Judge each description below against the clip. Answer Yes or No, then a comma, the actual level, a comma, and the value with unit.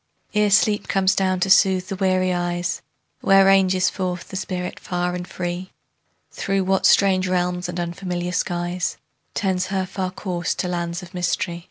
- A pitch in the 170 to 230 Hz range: Yes, medium, 185 Hz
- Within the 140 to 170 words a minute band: Yes, average, 165 wpm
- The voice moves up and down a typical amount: No, narrow, 1.3 semitones